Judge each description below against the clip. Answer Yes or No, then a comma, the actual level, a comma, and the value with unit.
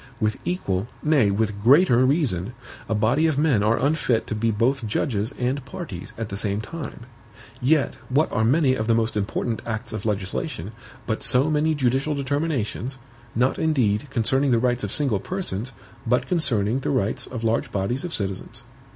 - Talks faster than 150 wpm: Yes, average, 175 wpm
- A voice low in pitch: Yes, low, 120 Hz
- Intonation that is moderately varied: Yes, average, 4.6 semitones